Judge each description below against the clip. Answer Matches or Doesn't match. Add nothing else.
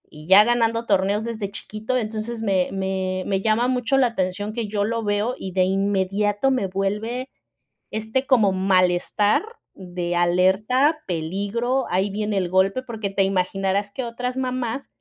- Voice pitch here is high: Matches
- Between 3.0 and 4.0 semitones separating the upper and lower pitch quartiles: Matches